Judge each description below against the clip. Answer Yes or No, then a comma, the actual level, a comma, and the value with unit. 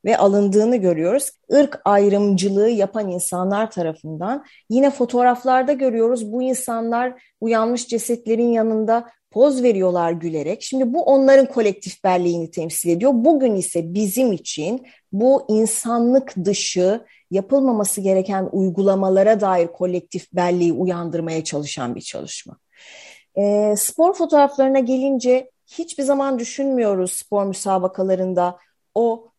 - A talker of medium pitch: No, high, 215 Hz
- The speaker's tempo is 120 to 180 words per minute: No, average, 110 wpm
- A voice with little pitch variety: No, average, 5.3 semitones